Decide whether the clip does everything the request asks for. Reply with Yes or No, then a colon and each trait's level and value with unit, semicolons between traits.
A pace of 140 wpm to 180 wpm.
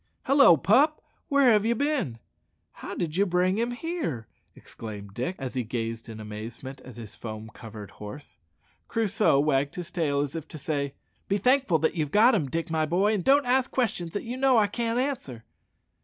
No: average, 190 wpm